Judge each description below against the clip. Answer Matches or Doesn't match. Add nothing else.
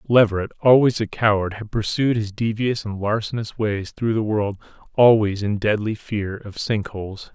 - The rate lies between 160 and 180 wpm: Matches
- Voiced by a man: Matches